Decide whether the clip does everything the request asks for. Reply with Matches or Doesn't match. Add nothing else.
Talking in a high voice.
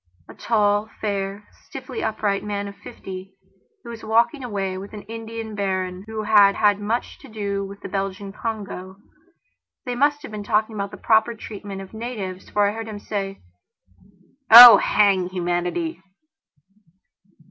Matches